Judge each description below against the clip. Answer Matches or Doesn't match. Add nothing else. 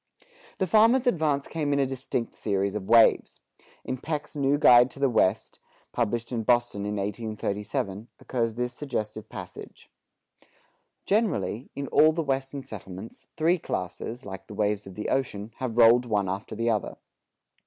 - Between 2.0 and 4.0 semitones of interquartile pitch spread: Doesn't match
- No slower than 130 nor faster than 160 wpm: Matches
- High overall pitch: Doesn't match